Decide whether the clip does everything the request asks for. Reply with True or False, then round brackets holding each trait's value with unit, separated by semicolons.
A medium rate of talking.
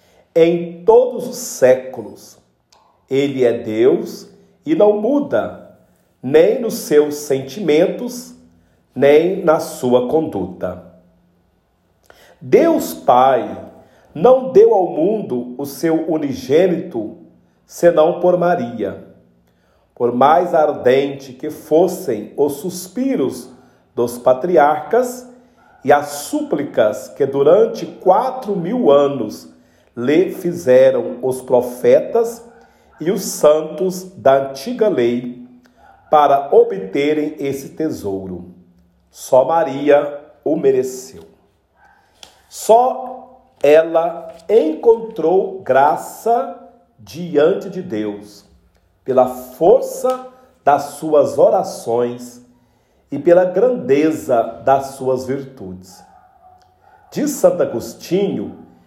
False (90 wpm)